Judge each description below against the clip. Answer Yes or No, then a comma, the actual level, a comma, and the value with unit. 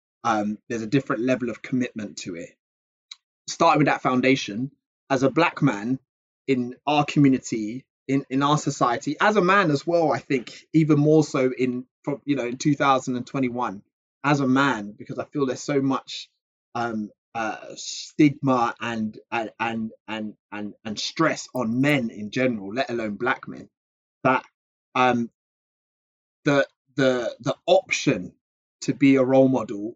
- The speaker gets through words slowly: No, average, 155 wpm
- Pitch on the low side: Yes, low, 130 Hz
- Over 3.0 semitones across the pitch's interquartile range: No, average, 2.7 semitones